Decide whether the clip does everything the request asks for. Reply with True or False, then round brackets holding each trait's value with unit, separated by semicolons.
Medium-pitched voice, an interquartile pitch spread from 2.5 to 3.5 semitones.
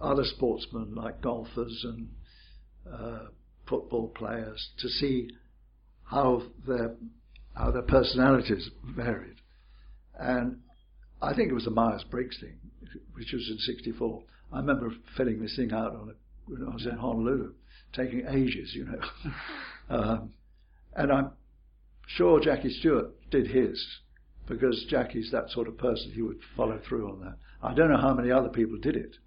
False (115 Hz; 2.9 semitones)